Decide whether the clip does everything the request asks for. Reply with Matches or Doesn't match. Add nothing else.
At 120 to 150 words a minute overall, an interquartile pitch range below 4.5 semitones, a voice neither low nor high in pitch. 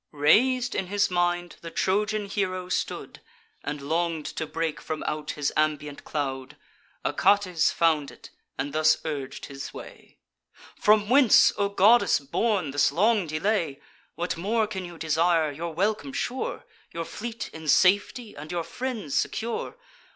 Doesn't match